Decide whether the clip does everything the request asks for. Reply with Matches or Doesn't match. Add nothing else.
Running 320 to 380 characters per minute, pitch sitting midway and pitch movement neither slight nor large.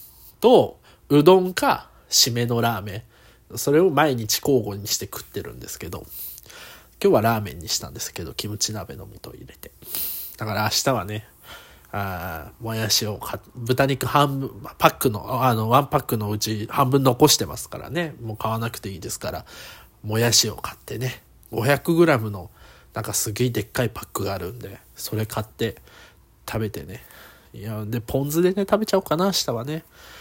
Doesn't match